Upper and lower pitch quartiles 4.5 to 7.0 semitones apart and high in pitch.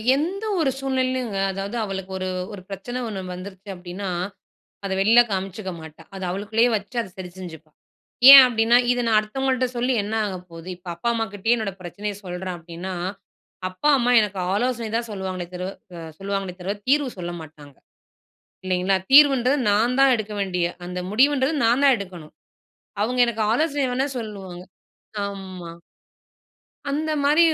Yes: average, 5.0 semitones; high, 205 Hz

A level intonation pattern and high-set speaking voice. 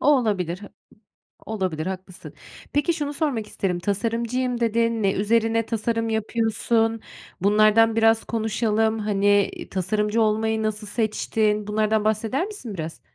Yes: narrow, 1.7 semitones; high, 220 Hz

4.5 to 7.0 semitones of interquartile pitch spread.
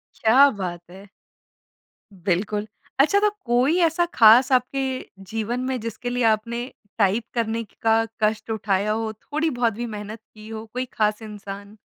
No: average, 2.9 semitones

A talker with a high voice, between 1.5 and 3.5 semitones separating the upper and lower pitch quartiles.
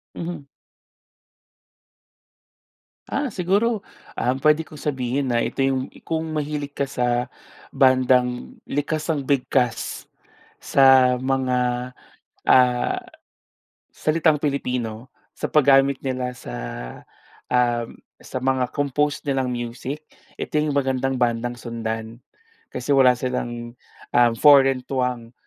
No: low, 130 Hz; narrow, 2.5 semitones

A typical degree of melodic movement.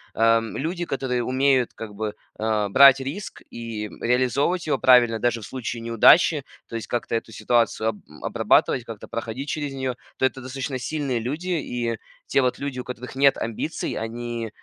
Yes: average, 3.1 semitones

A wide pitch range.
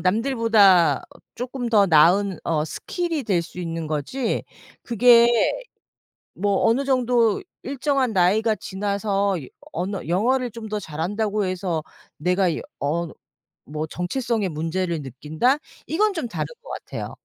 Yes: wide, 5.7 semitones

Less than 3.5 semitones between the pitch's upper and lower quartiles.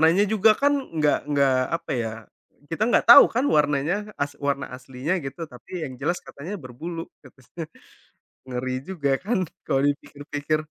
No: average, 4.2 semitones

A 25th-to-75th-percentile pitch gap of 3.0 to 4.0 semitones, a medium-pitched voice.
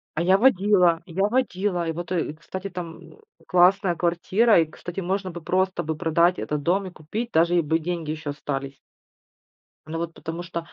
No: narrow, 2.5 semitones; medium, 175 Hz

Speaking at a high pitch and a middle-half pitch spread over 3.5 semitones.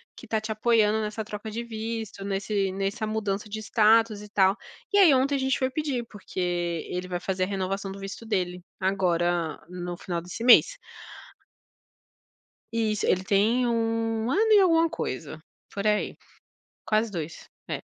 No: high, 215 Hz; average, 3.0 semitones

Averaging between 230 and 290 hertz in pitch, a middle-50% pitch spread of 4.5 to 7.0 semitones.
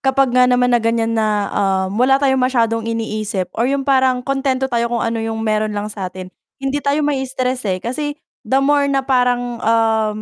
No: high, 245 Hz; average, 3.2 semitones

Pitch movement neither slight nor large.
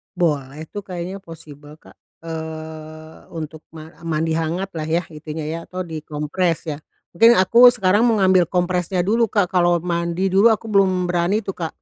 Yes: average, 3.1 semitones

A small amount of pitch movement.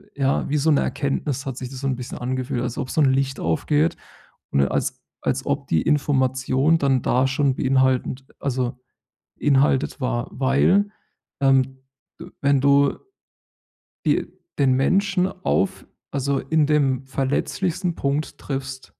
Yes: narrow, 1.9 semitones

